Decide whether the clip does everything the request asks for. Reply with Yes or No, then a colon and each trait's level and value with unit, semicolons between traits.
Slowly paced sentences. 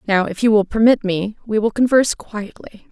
No: fast, 205 wpm